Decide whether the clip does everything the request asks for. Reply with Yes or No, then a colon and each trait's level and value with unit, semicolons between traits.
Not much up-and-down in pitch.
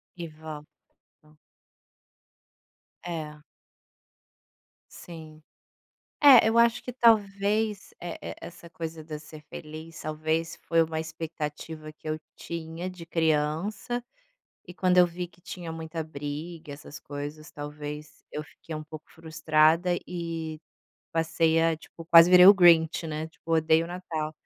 Yes: narrow, 2.0 semitones